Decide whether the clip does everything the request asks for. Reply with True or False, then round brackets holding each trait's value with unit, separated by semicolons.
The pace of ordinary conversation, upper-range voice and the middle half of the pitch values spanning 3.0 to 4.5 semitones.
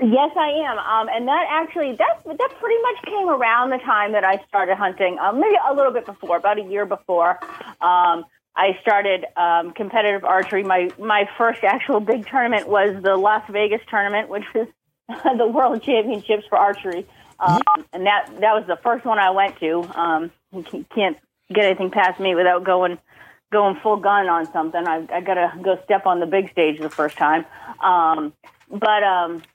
True (185 wpm; 200 Hz; 3.8 semitones)